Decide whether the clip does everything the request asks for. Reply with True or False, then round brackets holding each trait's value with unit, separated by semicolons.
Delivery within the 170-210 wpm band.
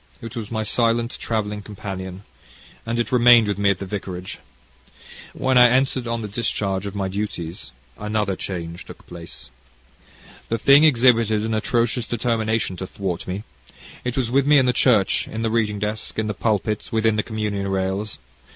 True (175 wpm)